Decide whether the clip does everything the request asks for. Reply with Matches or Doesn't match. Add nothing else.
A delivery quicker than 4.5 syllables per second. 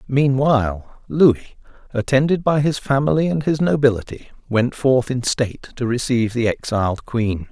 Matches